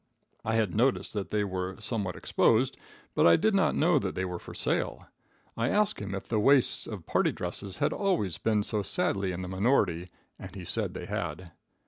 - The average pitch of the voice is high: No, low, 100 Hz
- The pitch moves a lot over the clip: No, average, 4.0 semitones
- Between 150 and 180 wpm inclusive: No, average, 200 wpm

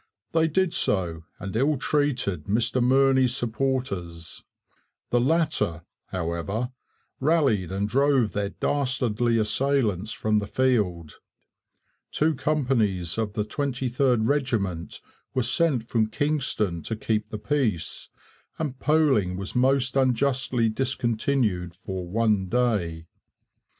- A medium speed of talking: No, slow, 110 wpm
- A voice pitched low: Yes, low, 120 Hz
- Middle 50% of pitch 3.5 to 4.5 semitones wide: No, average, 5.3 semitones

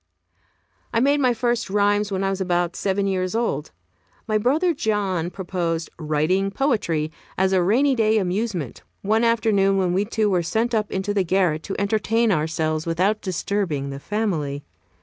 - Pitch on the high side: Yes, high, 195 Hz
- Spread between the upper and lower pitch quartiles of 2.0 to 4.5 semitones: Yes, average, 3.9 semitones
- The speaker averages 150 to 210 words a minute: Yes, average, 165 wpm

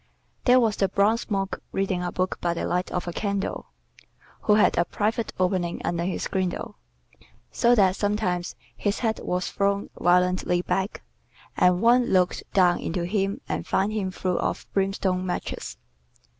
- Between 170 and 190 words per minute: No, average, 160 wpm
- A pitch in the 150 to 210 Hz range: Yes, high, 190 Hz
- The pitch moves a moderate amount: No, narrow, 2.3 semitones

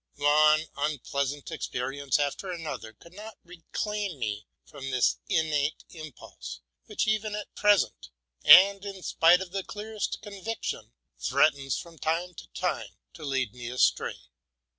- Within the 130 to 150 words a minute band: Yes, average, 140 wpm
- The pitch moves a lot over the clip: Yes, wide, 5.9 semitones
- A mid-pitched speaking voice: Yes, medium, 155 Hz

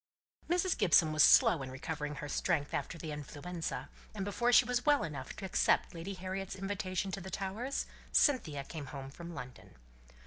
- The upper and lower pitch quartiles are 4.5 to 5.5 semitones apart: Yes, average, 5.0 semitones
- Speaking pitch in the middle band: Yes, medium, 175 Hz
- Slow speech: No, average, 175 wpm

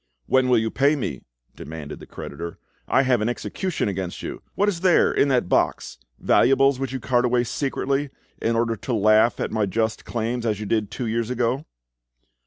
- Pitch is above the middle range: No, low, 120 Hz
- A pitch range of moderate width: Yes, average, 3.5 semitones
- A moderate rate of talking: Yes, average, 195 wpm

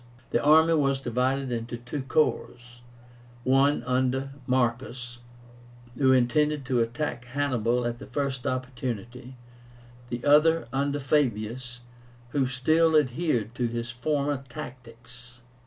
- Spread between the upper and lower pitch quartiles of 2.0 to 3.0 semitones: Yes, narrow, 2.6 semitones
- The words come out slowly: Yes, slow, 115 wpm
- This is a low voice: Yes, low, 130 Hz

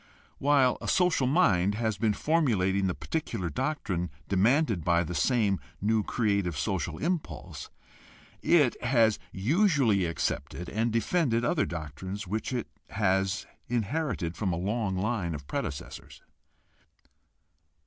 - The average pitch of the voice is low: Yes, low, 105 Hz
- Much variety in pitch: Yes, wide, 5.7 semitones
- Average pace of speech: No, slow, 120 wpm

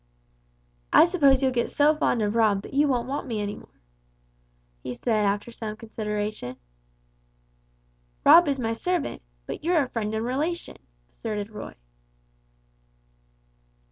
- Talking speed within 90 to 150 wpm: Yes, average, 140 wpm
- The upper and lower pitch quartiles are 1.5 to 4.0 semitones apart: No, average, 4.9 semitones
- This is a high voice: Yes, high, 230 Hz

